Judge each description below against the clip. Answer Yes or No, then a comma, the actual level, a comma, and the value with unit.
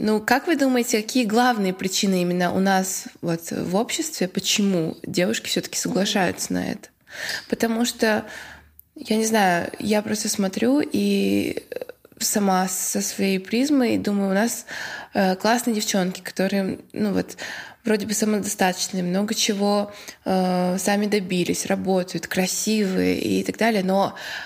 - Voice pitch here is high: Yes, high, 205 Hz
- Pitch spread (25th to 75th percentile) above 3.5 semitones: No, average, 3.2 semitones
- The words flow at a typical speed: Yes, average, 135 wpm